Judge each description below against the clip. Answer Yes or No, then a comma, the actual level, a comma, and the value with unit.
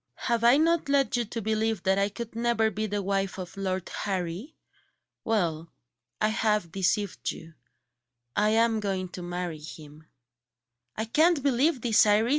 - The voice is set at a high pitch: Yes, high, 210 Hz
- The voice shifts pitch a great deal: No, average, 3.9 semitones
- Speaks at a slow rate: No, average, 160 wpm